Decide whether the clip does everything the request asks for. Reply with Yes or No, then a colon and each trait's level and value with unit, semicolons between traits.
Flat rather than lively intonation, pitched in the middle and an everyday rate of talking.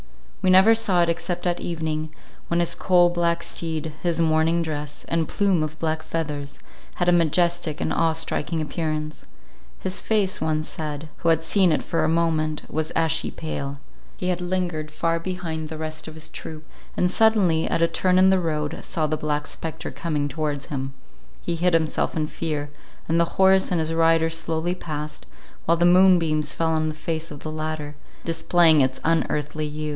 Yes: narrow, 1.9 semitones; medium, 160 Hz; average, 185 wpm